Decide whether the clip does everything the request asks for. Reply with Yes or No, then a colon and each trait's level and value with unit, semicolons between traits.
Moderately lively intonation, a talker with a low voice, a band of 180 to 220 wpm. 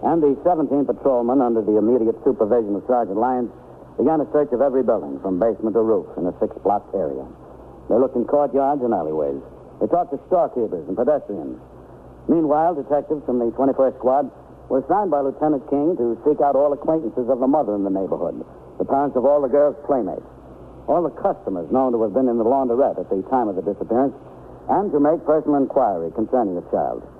Yes: average, 4.4 semitones; low, 130 Hz; average, 200 wpm